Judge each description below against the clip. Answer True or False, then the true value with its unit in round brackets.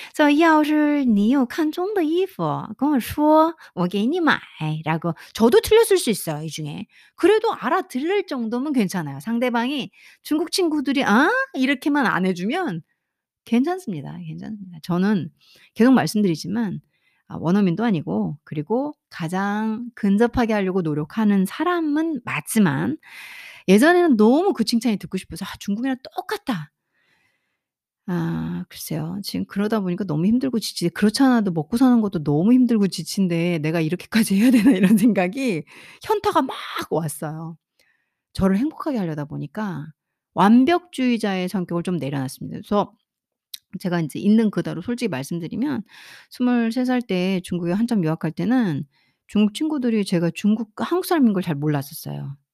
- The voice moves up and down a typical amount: False (7.4 semitones)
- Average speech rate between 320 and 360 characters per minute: True (330 characters per minute)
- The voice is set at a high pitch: True (215 Hz)